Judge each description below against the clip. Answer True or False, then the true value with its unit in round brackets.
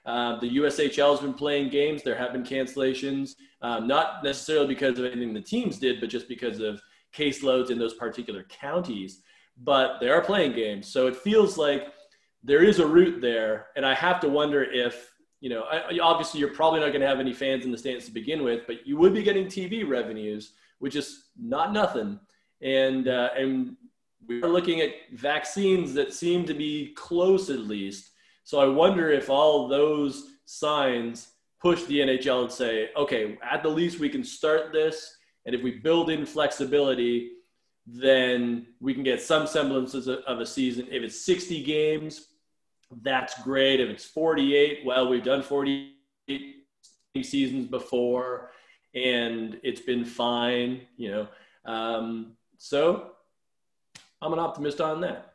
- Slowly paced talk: False (170 wpm)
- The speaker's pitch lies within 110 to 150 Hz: True (140 Hz)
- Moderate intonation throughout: True (4.3 semitones)